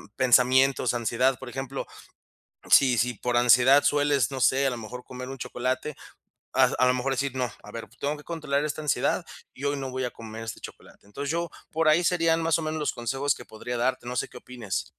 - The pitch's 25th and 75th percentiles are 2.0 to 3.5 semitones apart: Yes, average, 2.7 semitones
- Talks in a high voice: No, low, 130 Hz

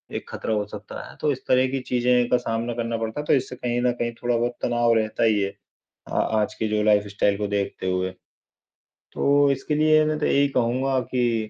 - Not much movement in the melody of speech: No, average, 3.0 semitones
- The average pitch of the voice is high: No, low, 120 Hz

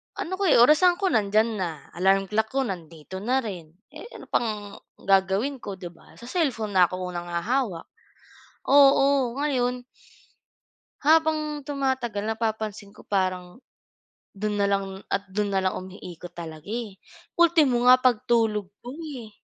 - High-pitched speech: Yes, high, 215 Hz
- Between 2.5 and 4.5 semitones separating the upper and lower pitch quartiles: No, wide, 5.6 semitones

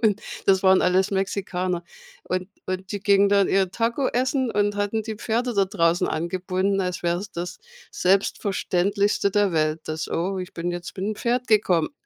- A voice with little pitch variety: Yes, narrow, 2.2 semitones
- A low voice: No, high, 195 Hz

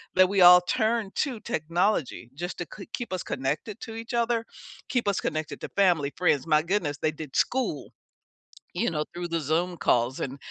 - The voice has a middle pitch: Yes, medium, 175 Hz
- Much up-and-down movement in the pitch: Yes, wide, 5.8 semitones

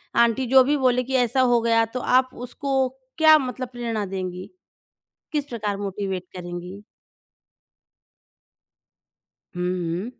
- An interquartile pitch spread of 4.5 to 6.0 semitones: Yes, average, 5.1 semitones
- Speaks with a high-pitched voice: Yes, high, 235 Hz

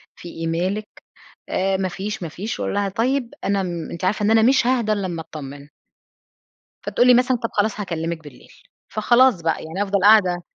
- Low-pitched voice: No, high, 195 Hz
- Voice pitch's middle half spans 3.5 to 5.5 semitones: Yes, average, 4.5 semitones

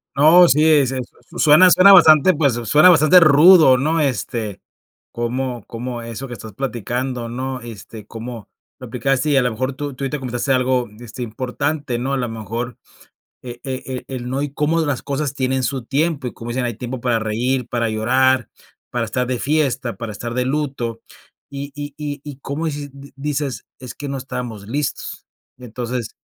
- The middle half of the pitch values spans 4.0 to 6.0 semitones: No, average, 3.1 semitones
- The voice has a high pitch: No, low, 130 Hz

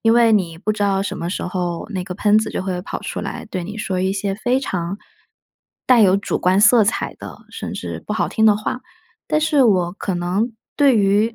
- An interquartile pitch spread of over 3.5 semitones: No, average, 3.2 semitones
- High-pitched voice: Yes, high, 200 Hz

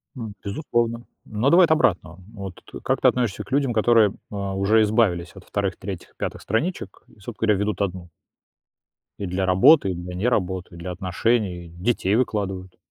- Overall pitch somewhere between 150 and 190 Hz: No, low, 100 Hz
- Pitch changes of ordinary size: Yes, average, 4.1 semitones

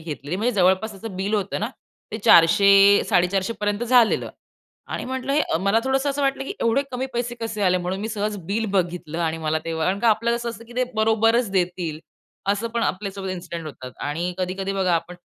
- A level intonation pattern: No, average, 4.3 semitones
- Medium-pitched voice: No, high, 200 Hz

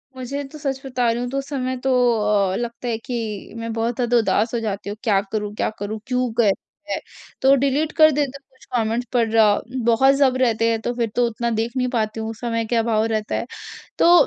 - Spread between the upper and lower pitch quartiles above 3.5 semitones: No, average, 2.7 semitones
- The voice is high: Yes, high, 235 Hz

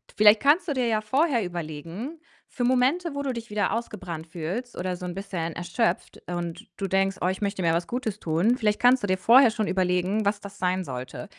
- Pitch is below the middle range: No, high, 200 Hz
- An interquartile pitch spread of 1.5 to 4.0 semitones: No, average, 5.3 semitones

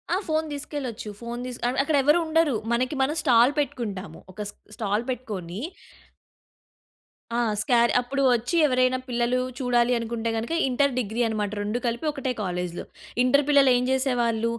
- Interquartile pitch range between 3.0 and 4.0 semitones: Yes, average, 3.3 semitones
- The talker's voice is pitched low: No, high, 245 Hz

